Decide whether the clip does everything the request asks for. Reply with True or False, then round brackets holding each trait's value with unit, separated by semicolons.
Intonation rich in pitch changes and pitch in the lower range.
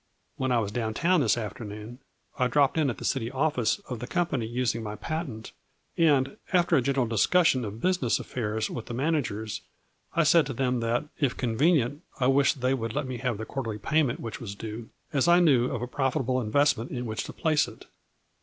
False (4.1 semitones; 125 Hz)